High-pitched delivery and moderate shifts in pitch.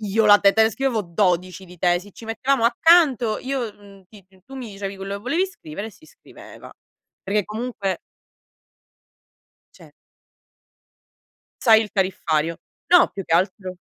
Yes: high, 205 Hz; average, 3.6 semitones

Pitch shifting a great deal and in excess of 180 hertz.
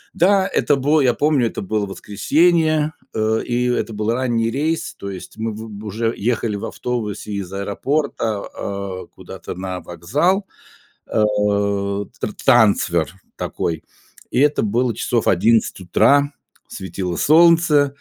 No: wide, 6.1 semitones; low, 115 Hz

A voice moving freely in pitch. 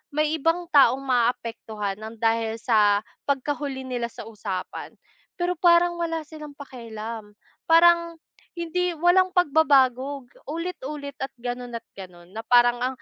Yes: wide, 6.1 semitones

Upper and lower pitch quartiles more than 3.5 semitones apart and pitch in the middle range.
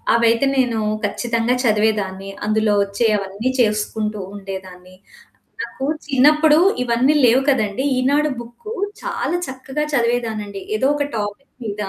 No: average, 4.1 semitones; high, 230 Hz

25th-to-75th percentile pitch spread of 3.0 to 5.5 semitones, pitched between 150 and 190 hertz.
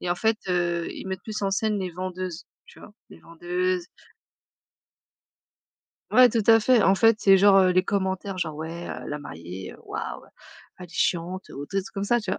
No: narrow, 2.5 semitones; medium, 185 Hz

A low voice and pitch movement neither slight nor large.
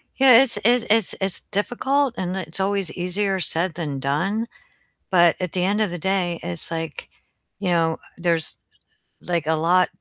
No: medium, 180 Hz; average, 3.5 semitones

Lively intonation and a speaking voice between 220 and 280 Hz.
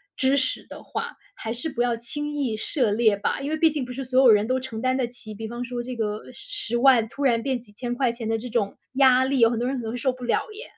No: narrow, 2.5 semitones; high, 245 Hz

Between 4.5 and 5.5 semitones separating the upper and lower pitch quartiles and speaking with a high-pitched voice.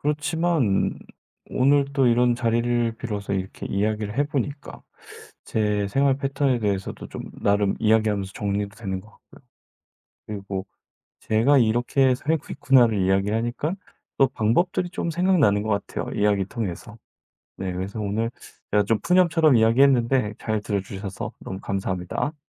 No: average, 5.1 semitones; low, 110 Hz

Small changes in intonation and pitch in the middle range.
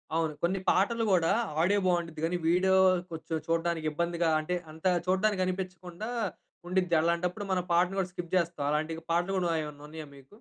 Yes: narrow, 2.1 semitones; medium, 175 Hz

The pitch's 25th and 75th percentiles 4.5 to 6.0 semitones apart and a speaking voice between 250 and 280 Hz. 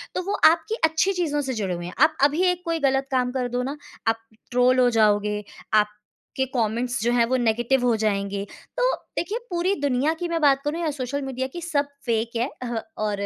Yes: wide, 5.6 semitones; very high, 260 Hz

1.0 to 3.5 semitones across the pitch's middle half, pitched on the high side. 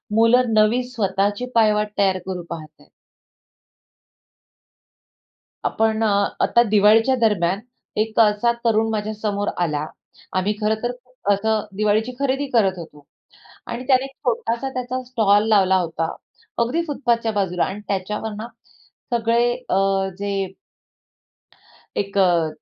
Yes: average, 2.9 semitones; high, 215 Hz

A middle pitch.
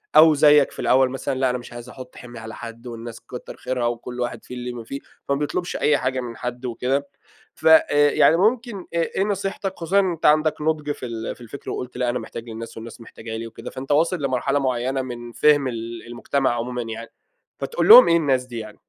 No: low, 125 Hz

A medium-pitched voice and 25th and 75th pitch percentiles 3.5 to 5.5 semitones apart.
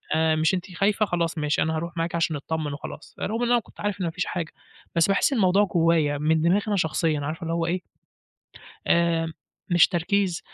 No: medium, 170 Hz; narrow, 2.6 semitones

